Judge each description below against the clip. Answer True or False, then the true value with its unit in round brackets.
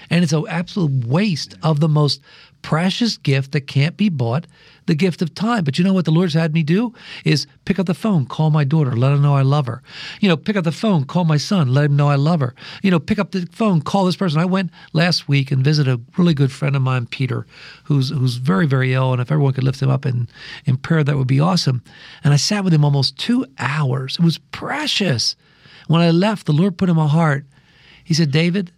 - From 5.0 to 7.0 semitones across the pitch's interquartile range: False (4.2 semitones)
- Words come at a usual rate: False (250 wpm)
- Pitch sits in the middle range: True (155 Hz)